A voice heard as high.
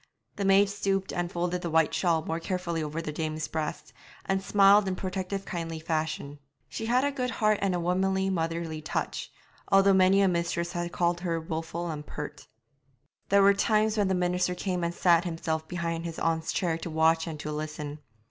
No: medium, 175 Hz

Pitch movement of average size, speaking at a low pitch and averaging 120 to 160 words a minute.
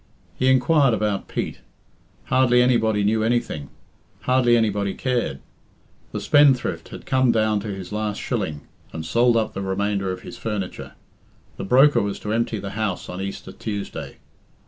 Yes: average, 3.7 semitones; low, 110 Hz; average, 155 wpm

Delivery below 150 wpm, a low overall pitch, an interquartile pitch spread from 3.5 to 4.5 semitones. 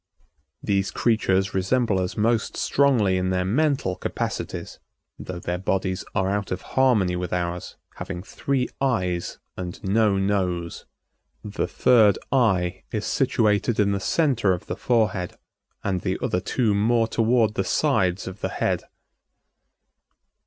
Yes: average, 140 wpm; low, 100 Hz; average, 3.8 semitones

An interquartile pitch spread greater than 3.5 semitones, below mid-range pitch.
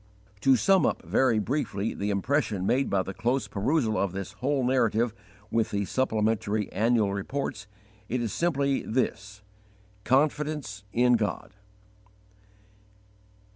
Yes: average, 4.7 semitones; low, 115 Hz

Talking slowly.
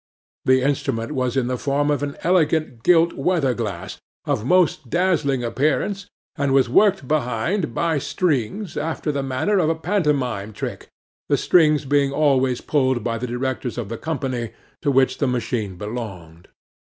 No: average, 160 wpm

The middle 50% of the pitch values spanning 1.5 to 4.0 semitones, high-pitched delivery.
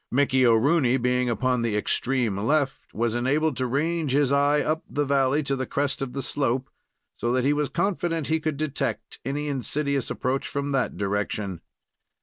No: average, 2.9 semitones; low, 135 Hz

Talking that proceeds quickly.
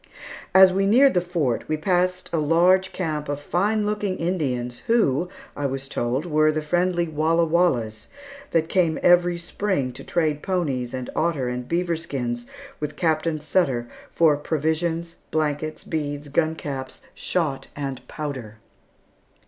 No: average, 145 wpm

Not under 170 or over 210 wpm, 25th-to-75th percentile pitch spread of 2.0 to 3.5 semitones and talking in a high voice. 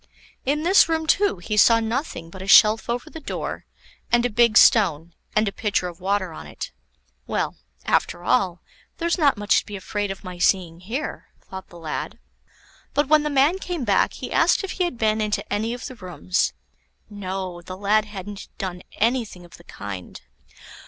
No: average, 190 wpm; average, 5.1 semitones; high, 210 Hz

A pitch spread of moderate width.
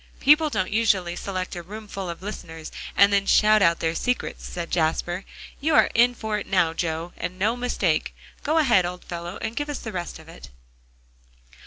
Yes: average, 4.4 semitones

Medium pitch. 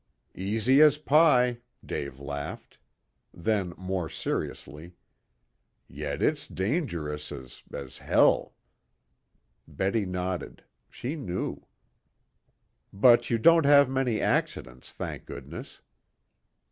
No: very low, 95 Hz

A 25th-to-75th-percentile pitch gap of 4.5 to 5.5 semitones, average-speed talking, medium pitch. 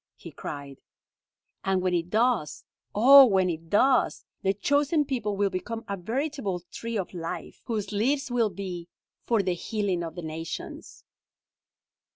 No: average, 5.1 semitones; average, 150 wpm; high, 200 Hz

